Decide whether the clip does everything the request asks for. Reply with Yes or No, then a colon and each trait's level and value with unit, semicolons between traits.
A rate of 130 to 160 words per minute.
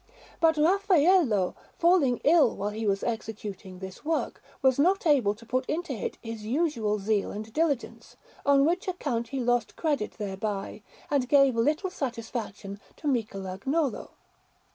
Yes: average, 140 wpm